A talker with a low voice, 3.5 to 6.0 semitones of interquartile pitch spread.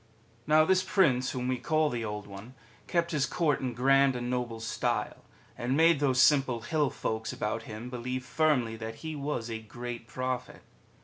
Yes: low, 125 Hz; average, 4.2 semitones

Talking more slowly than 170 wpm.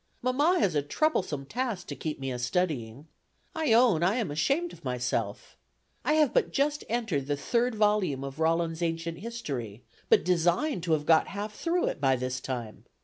No: average, 185 wpm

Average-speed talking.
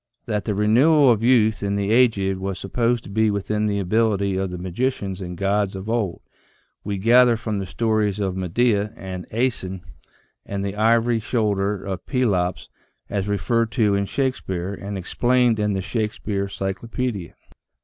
Yes: average, 170 wpm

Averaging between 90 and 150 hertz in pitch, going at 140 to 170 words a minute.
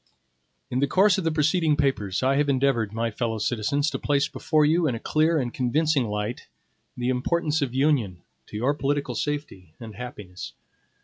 No: low, 135 Hz; average, 180 wpm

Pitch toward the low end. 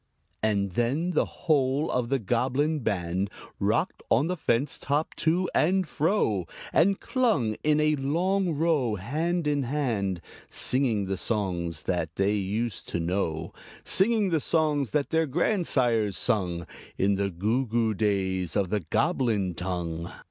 Yes: low, 120 Hz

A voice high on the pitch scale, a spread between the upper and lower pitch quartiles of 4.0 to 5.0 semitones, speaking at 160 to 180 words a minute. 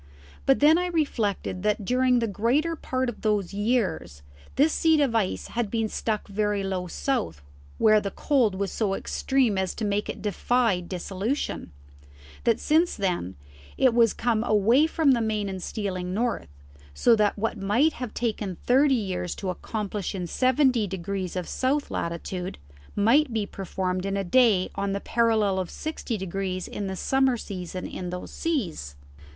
Yes: high, 210 Hz; average, 4.6 semitones; average, 170 wpm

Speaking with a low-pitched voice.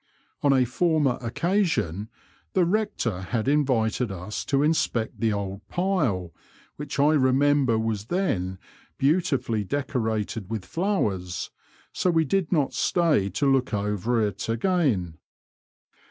Yes: low, 125 Hz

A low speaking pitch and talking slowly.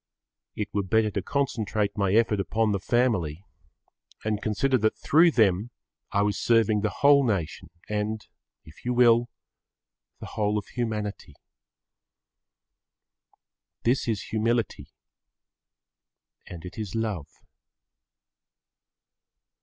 Yes: low, 110 Hz; slow, 110 wpm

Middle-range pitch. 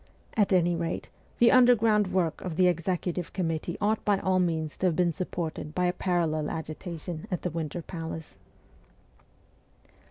Yes: medium, 175 Hz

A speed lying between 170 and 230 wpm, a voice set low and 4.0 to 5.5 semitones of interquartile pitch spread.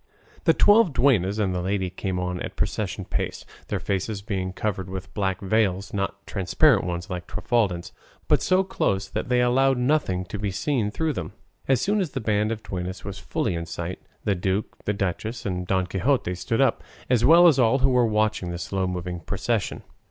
Yes: average, 195 wpm; low, 100 Hz; average, 4.9 semitones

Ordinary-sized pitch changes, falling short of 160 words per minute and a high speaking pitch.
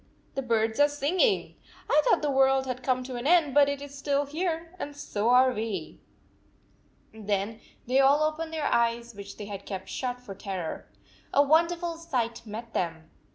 No: average, 4.8 semitones; average, 180 wpm; very high, 260 Hz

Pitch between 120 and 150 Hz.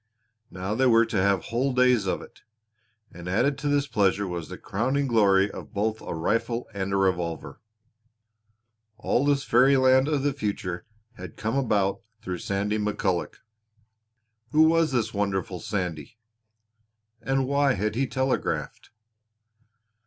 No: low, 110 Hz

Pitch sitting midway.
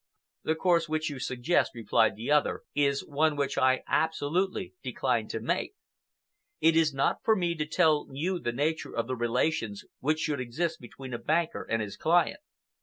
Yes: medium, 150 Hz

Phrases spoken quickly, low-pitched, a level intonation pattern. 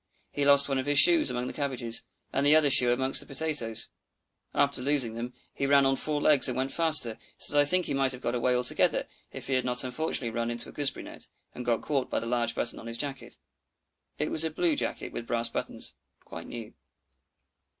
No: fast, 225 wpm; low, 130 Hz; average, 3.2 semitones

